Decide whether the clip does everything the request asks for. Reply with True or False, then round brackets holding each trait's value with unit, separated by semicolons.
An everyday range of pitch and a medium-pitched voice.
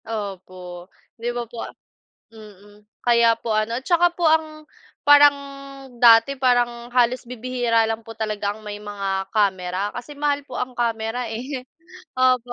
False (3.2 semitones; 230 Hz)